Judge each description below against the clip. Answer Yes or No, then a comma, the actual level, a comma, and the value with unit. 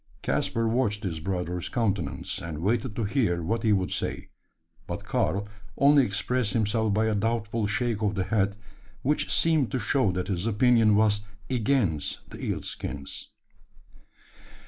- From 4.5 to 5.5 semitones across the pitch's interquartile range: No, average, 3.2 semitones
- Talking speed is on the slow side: No, average, 150 wpm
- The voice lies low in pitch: Yes, low, 105 Hz